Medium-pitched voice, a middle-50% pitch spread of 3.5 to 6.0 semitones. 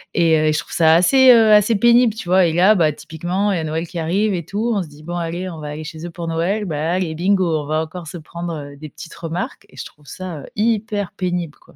Yes: medium, 175 Hz; average, 3.8 semitones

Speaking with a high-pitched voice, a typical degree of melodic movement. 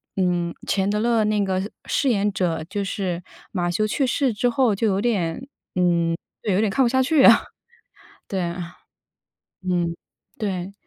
Yes: high, 195 Hz; average, 4.1 semitones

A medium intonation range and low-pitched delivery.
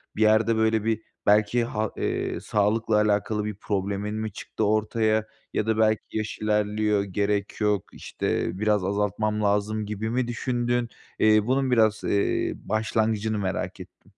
No: narrow, 1.1 semitones; low, 110 Hz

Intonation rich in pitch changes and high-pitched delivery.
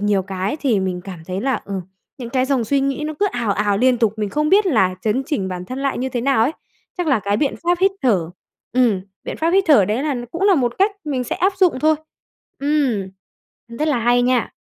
Yes: wide, 6.4 semitones; very high, 255 Hz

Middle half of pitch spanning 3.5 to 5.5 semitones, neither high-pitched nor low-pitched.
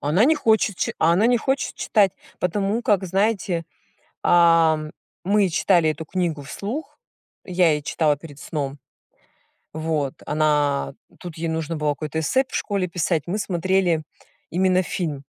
Yes: average, 3.9 semitones; medium, 170 Hz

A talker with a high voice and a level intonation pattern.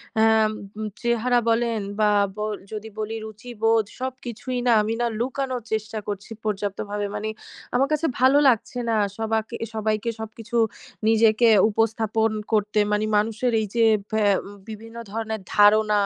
Yes: high, 220 Hz; narrow, 1.8 semitones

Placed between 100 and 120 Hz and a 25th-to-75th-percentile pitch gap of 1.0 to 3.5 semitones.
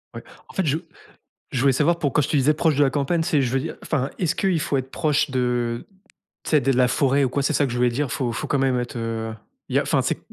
No: low, 135 Hz; average, 3.2 semitones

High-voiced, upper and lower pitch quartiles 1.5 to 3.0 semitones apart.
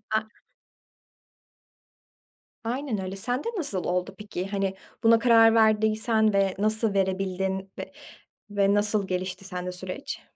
Yes: high, 200 Hz; narrow, 2.5 semitones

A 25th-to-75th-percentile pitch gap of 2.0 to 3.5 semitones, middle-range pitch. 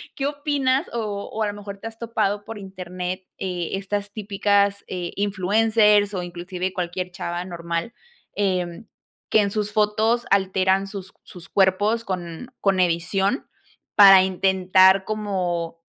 No: narrow, 2.5 semitones; high, 195 Hz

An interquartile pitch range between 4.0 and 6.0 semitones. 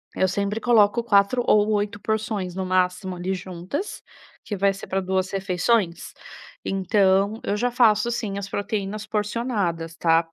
No: narrow, 2.4 semitones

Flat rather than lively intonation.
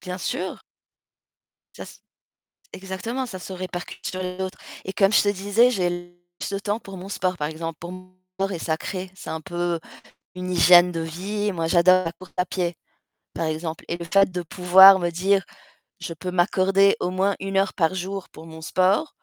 Yes: narrow, 2.0 semitones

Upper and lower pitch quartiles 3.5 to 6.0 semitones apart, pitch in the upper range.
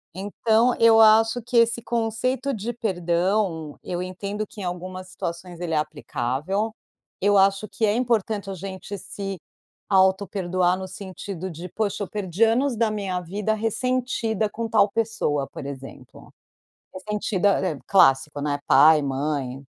Yes: average, 4.0 semitones; high, 195 Hz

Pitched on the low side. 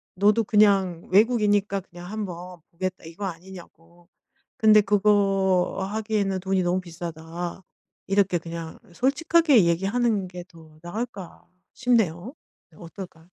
No: high, 190 Hz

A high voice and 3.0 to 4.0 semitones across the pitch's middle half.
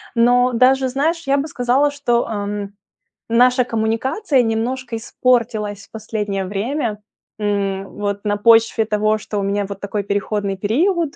Yes: high, 225 Hz; average, 3.6 semitones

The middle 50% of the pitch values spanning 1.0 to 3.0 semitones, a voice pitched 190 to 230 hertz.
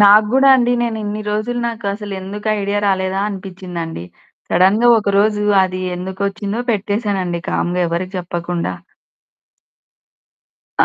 Yes: narrow, 2.4 semitones; high, 200 Hz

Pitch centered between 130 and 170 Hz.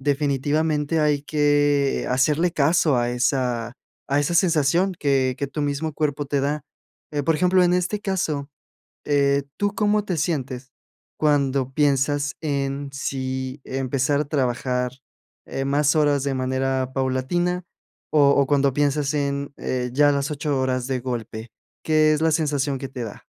Yes: medium, 140 Hz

